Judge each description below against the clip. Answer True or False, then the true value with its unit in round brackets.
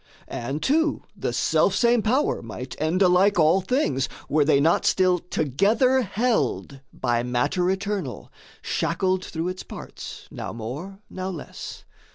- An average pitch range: False (5.8 semitones)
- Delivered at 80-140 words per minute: True (135 wpm)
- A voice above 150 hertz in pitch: True (185 Hz)